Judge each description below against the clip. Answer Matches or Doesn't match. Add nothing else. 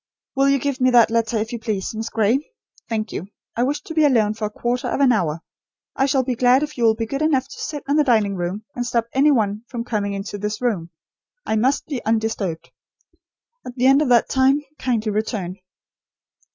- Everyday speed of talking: Doesn't match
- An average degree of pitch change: Matches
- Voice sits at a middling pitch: Doesn't match